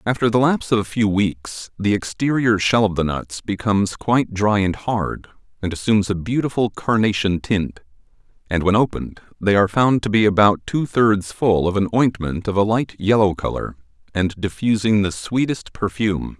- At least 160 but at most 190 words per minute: Yes, average, 180 wpm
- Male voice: Yes, male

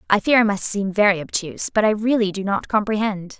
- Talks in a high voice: Yes, high, 205 Hz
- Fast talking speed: Yes, fast, 230 wpm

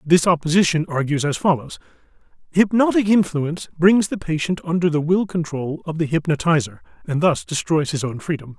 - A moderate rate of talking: Yes, average, 160 wpm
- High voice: No, medium, 165 Hz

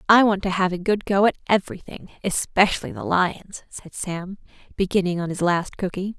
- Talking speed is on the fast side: No, average, 195 wpm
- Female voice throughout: Yes, female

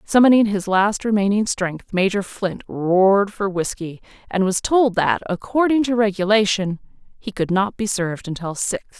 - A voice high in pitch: Yes, high, 200 Hz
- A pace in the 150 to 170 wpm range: Yes, average, 160 wpm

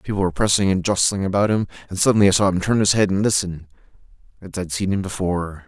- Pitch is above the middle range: No, very low, 95 Hz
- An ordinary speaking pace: No, fast, 235 wpm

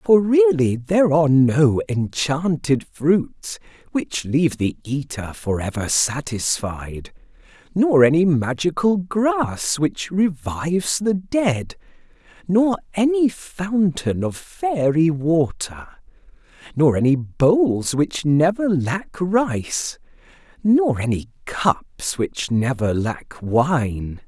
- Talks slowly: Yes, slow, 90 wpm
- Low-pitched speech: No, medium, 160 Hz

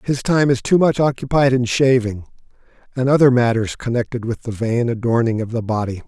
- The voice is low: Yes, low, 125 Hz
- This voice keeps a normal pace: Yes, average, 190 wpm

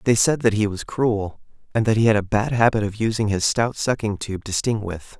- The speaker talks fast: Yes, fast, 255 wpm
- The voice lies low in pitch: Yes, low, 110 Hz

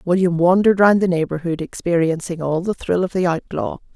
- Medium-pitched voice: Yes, medium, 175 Hz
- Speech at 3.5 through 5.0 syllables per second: No, 5.6 syllables/s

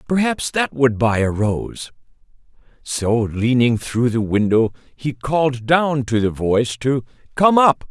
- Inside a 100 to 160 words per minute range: Yes, average, 150 wpm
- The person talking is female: No, male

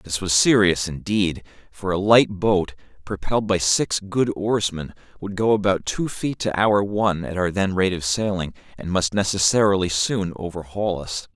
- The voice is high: No, very low, 95 Hz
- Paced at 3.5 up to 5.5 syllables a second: Yes, 4.6 syllables/s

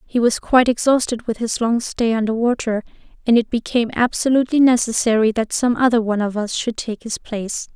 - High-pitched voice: Yes, high, 230 Hz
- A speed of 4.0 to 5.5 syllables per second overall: No, 5.9 syllables/s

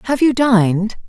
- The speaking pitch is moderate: No, high, 230 Hz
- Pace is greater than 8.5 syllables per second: No, 4.8 syllables/s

